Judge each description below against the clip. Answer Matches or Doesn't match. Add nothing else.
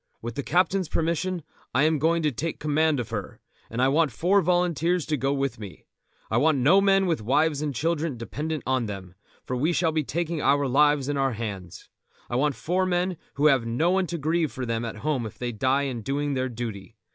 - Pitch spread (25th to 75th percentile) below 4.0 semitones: Doesn't match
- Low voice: Doesn't match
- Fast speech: Matches